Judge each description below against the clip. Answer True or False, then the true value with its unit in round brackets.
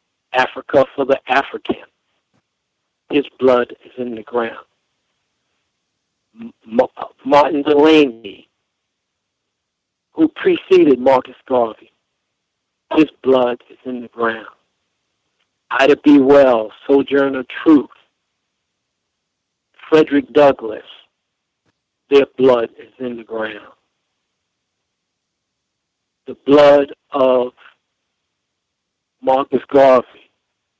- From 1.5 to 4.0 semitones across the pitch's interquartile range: True (2.7 semitones)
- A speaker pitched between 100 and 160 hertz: True (135 Hz)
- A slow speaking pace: True (80 wpm)